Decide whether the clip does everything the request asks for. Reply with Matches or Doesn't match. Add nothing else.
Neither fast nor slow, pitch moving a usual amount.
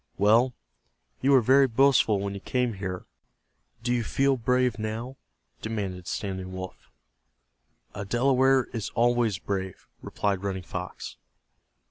Doesn't match